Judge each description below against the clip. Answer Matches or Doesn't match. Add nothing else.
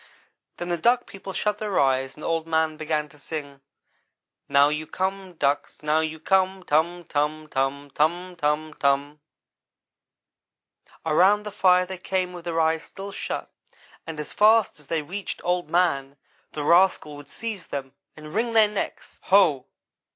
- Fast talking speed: Doesn't match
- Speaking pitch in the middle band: Matches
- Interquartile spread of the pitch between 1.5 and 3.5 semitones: Doesn't match